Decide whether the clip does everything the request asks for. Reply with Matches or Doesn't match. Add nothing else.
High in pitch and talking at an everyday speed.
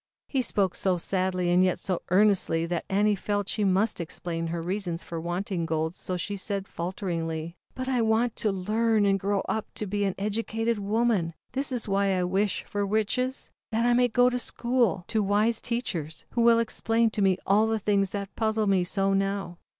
Matches